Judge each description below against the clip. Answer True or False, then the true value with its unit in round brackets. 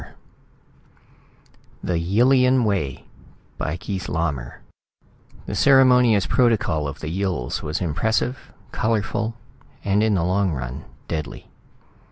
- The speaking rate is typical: False (110 wpm)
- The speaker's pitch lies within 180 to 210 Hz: False (95 Hz)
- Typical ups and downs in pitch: False (6.4 semitones)